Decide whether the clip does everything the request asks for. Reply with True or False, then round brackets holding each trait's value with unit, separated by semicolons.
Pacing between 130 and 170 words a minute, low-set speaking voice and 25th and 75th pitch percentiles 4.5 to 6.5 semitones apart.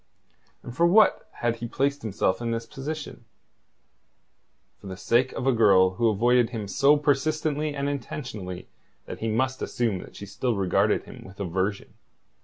True (165 wpm; 120 Hz; 5.6 semitones)